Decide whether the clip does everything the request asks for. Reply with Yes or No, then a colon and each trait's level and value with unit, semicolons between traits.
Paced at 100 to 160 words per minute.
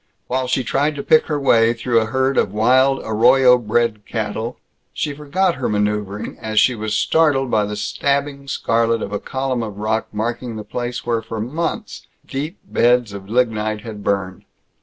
No: average, 180 wpm